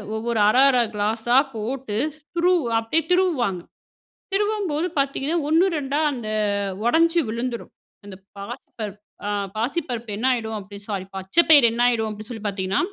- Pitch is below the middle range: No, high, 240 Hz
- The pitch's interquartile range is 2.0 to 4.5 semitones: No, wide, 5.5 semitones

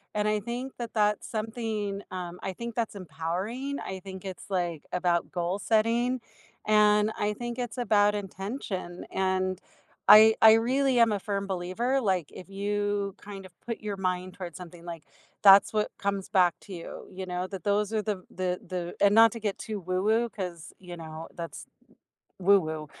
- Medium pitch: No, high, 200 Hz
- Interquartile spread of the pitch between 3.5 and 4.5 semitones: No, average, 3.1 semitones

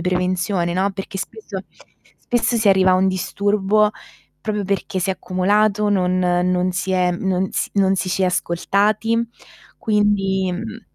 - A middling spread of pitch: No, narrow, 2.2 semitones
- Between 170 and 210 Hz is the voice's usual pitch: Yes, high, 190 Hz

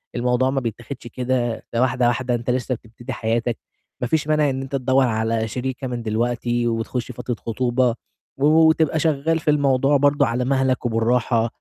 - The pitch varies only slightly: Yes, narrow, 2.2 semitones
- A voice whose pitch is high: No, low, 125 Hz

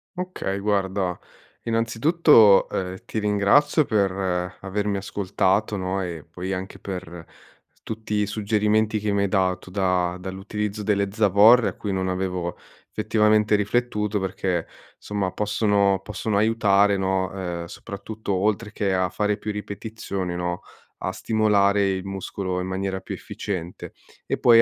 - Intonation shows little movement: Yes, narrow, 2.2 semitones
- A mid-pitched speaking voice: No, low, 100 Hz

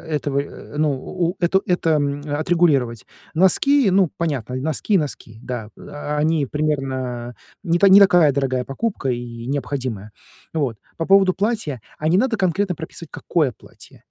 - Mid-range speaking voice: Yes, medium, 150 Hz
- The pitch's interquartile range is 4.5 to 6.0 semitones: Yes, average, 5.3 semitones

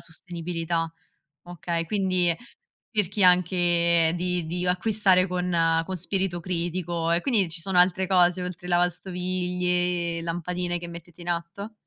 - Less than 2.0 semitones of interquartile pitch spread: Yes, narrow, 1.2 semitones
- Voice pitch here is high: No, medium, 180 Hz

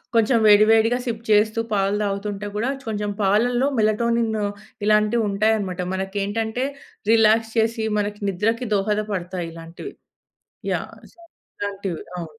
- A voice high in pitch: Yes, high, 210 Hz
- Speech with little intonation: Yes, narrow, 2.2 semitones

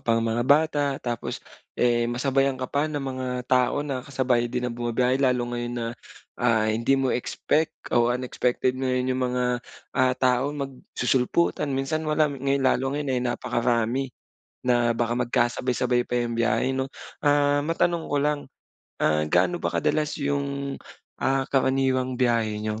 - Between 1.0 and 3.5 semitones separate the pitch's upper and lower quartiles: Yes, narrow, 2.4 semitones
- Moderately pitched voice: No, low, 130 Hz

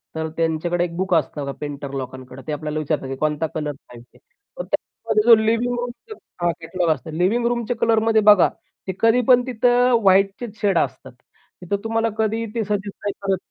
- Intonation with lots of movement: Yes, wide, 6.6 semitones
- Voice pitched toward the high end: Yes, high, 195 Hz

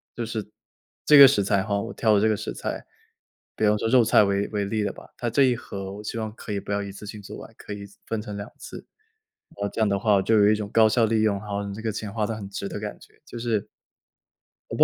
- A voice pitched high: No, low, 105 Hz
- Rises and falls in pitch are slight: Yes, narrow, 1.7 semitones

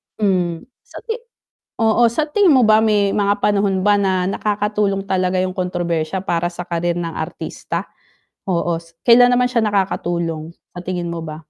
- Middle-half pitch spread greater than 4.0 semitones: No, average, 3.3 semitones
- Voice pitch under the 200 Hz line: Yes, high, 190 Hz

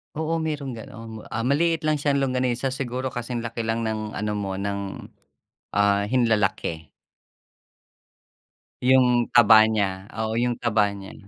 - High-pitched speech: No, low, 115 Hz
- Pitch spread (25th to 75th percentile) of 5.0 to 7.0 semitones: No, average, 3.7 semitones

